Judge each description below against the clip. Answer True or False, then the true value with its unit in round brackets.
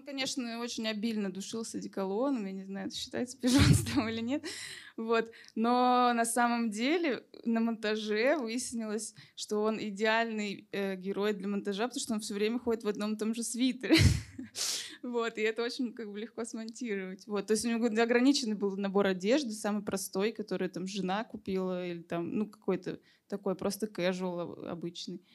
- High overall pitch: True (220 Hz)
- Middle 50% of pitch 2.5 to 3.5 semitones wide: True (3.0 semitones)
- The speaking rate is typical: False (170 wpm)